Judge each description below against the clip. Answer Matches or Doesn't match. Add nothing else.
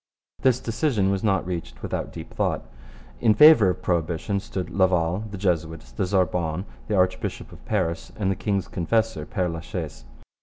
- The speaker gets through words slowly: Doesn't match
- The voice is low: Matches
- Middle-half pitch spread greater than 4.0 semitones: Doesn't match